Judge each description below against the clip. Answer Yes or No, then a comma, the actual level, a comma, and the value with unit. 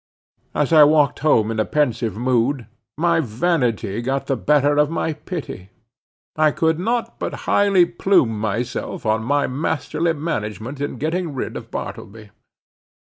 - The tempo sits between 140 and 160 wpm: Yes, average, 145 wpm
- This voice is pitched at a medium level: Yes, medium, 145 Hz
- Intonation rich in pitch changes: Yes, wide, 5.9 semitones